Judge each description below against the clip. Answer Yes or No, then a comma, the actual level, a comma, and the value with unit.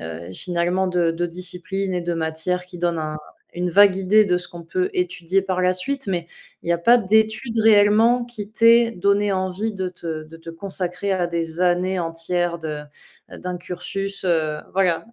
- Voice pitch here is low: No, medium, 180 Hz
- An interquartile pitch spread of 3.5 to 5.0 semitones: No, average, 2.9 semitones